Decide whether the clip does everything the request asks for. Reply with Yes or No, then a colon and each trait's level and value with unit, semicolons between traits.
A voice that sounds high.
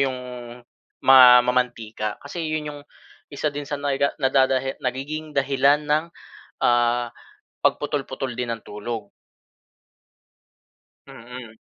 No: low, 130 Hz